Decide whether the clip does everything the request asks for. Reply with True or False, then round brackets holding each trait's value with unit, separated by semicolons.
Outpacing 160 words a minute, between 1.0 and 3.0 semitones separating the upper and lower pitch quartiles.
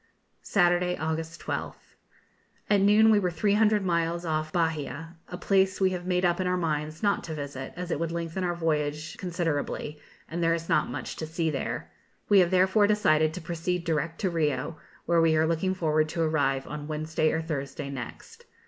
True (185 wpm; 2.6 semitones)